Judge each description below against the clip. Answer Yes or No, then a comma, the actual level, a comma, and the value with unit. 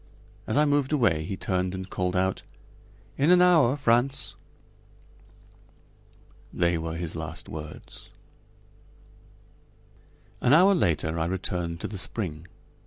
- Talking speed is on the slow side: Yes, slow, 120 wpm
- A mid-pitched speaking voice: No, very low, 95 Hz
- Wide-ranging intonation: Yes, wide, 8.4 semitones